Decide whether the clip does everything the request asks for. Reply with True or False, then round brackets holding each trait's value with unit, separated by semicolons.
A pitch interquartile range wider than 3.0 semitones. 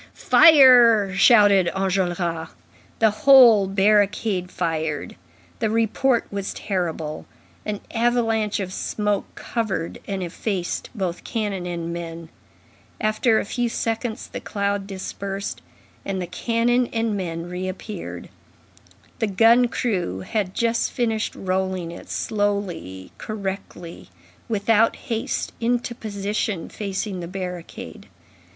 True (3.7 semitones)